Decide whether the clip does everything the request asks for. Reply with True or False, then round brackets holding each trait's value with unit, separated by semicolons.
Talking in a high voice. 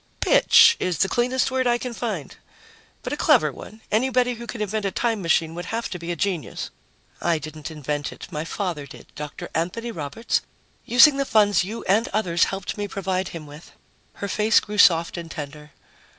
True (195 Hz)